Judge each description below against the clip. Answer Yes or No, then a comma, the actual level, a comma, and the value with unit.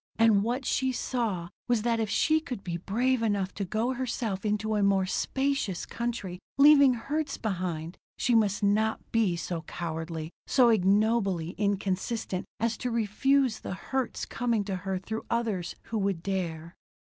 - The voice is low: No, high, 210 Hz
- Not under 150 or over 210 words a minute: Yes, average, 160 wpm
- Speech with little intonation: No, average, 4.1 semitones